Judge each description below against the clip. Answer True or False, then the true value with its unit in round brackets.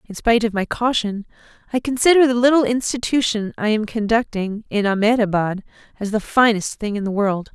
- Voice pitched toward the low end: False (220 Hz)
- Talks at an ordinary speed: True (175 wpm)